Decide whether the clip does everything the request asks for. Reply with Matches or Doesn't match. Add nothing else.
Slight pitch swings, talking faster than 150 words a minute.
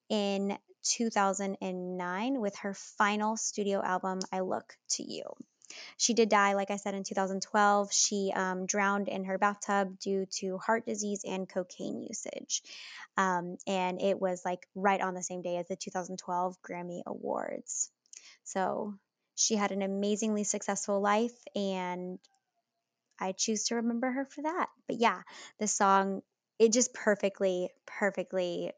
Doesn't match